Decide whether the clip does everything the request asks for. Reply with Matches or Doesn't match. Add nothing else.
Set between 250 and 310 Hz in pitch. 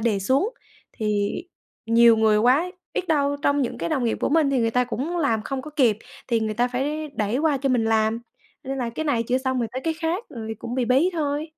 Matches